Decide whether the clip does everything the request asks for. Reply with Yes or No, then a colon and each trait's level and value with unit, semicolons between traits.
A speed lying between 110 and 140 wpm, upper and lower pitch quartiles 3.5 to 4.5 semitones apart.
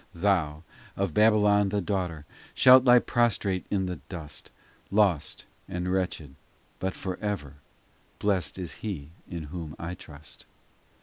Yes: slow, 135 wpm; average, 4.1 semitones